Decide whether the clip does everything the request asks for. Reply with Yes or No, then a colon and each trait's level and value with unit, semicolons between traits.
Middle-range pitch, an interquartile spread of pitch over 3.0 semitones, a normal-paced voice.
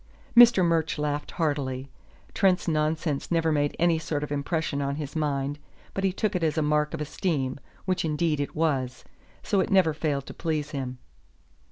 No: medium, 155 Hz; narrow, 2.6 semitones; average, 180 wpm